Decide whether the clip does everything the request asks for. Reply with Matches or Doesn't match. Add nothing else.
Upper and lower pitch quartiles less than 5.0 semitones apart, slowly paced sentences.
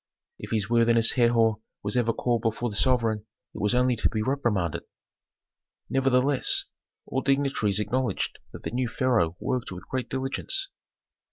Doesn't match